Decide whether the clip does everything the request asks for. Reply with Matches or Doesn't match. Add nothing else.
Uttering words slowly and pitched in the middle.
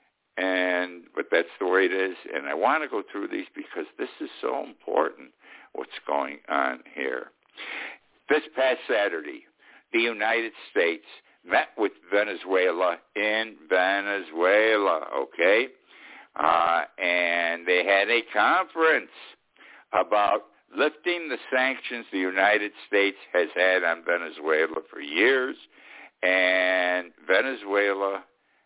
Doesn't match